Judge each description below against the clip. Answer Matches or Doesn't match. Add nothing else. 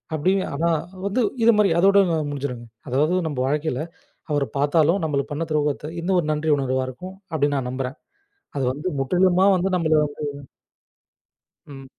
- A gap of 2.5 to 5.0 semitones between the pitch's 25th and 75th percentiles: Matches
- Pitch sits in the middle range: Matches